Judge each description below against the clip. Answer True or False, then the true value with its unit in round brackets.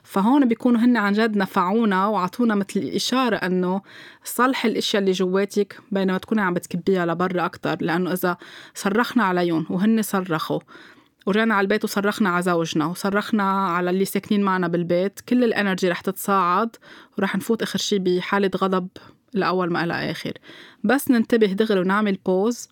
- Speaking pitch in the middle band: False (195 Hz)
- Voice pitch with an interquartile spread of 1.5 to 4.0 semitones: True (3.1 semitones)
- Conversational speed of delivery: False (150 wpm)